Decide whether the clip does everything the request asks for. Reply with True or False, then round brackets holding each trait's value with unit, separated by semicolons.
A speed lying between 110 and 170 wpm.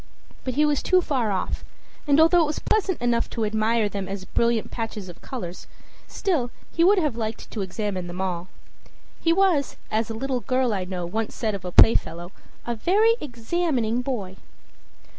False (180 wpm)